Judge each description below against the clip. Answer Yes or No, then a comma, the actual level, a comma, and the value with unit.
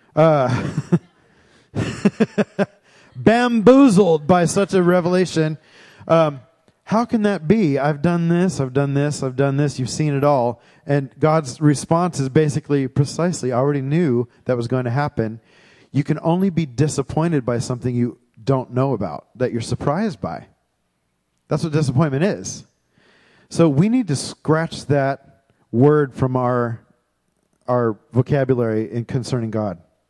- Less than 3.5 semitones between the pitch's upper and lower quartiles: No, average, 4.7 semitones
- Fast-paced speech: No, average, 140 wpm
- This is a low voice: No, medium, 145 Hz